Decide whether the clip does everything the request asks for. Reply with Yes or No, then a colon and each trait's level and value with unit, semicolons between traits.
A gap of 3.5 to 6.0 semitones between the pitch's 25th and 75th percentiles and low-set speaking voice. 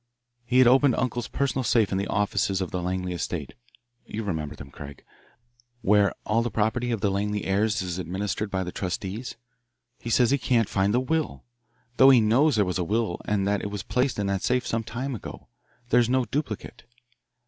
Yes: average, 4.1 semitones; low, 105 Hz